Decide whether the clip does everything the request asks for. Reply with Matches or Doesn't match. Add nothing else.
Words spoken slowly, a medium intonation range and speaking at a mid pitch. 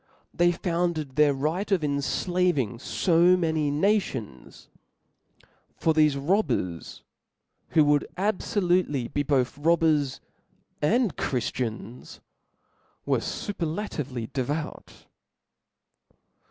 Matches